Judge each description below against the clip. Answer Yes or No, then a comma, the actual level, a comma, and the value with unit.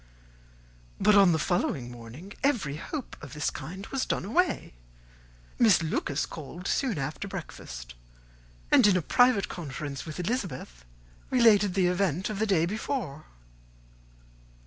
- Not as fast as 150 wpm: Yes, slow, 135 wpm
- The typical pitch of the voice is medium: Yes, medium, 180 Hz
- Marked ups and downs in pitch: Yes, wide, 6.0 semitones